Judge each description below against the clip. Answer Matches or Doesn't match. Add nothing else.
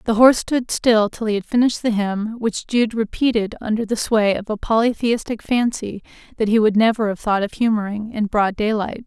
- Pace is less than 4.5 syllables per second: Doesn't match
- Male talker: Doesn't match